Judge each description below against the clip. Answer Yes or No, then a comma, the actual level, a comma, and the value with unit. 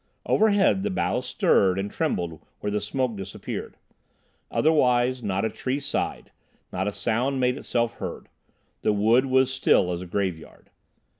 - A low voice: Yes, low, 115 Hz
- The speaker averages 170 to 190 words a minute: No, average, 150 wpm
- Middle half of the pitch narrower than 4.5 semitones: No, average, 5.2 semitones